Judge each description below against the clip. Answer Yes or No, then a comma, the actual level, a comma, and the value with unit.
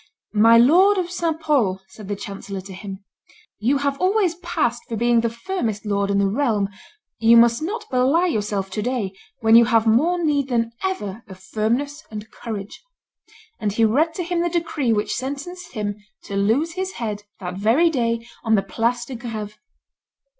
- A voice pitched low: No, high, 235 Hz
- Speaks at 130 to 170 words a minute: No, average, 180 wpm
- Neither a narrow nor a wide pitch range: No, wide, 6.6 semitones